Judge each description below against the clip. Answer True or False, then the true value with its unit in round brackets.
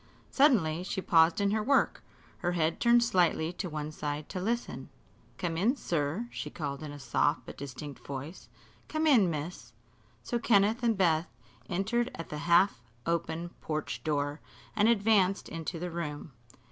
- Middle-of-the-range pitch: True (170 Hz)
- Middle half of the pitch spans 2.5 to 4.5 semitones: False (5.2 semitones)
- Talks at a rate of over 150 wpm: True (160 wpm)